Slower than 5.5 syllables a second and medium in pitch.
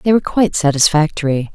No: 6.9 syllables/s; medium, 165 Hz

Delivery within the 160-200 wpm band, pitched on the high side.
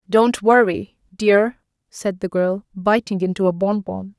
No: average, 145 wpm; high, 200 Hz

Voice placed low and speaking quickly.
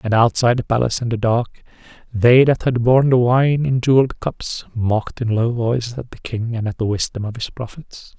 Yes: low, 120 Hz; fast, 220 wpm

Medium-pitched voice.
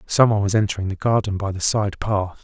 No: low, 100 Hz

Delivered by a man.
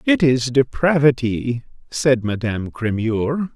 Yes: male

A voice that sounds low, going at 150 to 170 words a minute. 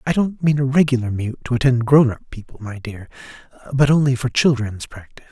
No: low, 125 Hz; fast, 205 wpm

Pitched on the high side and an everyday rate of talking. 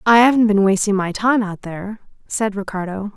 Yes: high, 205 Hz; average, 190 wpm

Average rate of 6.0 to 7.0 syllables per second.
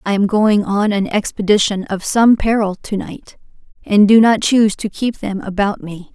No: 4.7 syllables/s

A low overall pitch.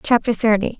No: high, 225 Hz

